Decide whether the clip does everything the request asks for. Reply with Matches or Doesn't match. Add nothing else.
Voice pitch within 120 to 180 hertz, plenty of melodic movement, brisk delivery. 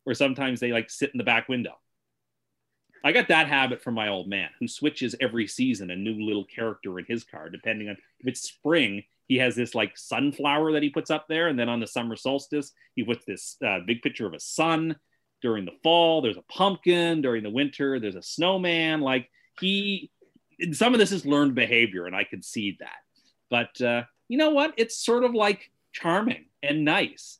Matches